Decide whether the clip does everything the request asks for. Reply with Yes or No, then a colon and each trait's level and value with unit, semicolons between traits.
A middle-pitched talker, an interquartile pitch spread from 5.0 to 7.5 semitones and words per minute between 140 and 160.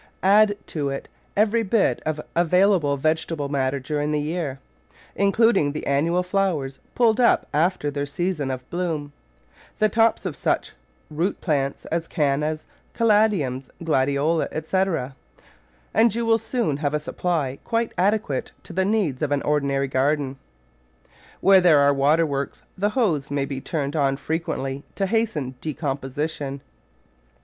Yes: medium, 155 Hz; wide, 5.4 semitones; average, 145 wpm